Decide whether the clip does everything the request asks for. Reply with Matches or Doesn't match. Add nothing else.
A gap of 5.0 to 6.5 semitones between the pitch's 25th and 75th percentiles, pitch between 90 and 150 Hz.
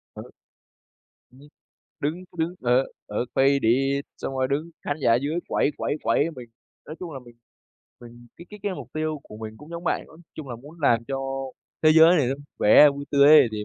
Doesn't match